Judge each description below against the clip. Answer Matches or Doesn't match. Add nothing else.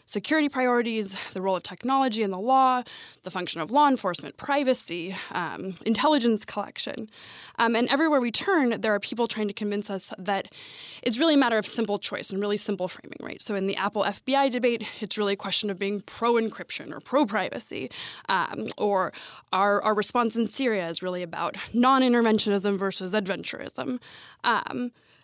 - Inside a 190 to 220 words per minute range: Doesn't match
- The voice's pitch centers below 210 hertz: Doesn't match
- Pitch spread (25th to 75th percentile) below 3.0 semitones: Doesn't match